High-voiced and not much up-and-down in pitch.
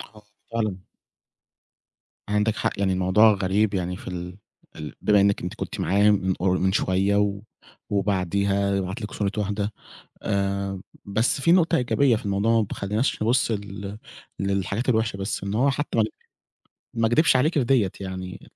No: low, 100 Hz; narrow, 2.3 semitones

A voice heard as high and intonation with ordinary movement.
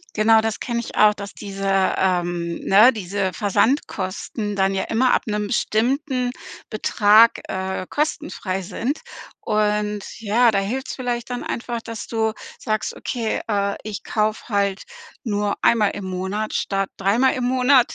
Yes: high, 215 Hz; average, 3.1 semitones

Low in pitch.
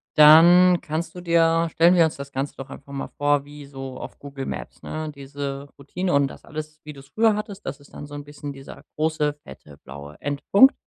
No: medium, 145 Hz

